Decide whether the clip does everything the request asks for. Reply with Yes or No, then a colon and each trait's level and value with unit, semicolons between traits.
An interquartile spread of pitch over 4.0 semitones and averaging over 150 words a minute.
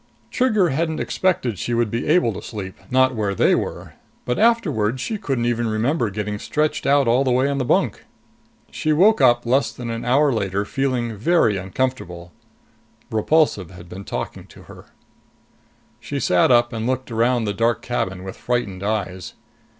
Yes: average, 4.8 semitones; average, 175 wpm